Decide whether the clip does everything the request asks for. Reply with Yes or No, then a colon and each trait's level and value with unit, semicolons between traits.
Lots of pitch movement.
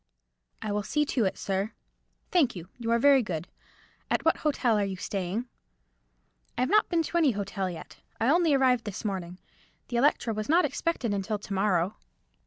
Yes: wide, 6.0 semitones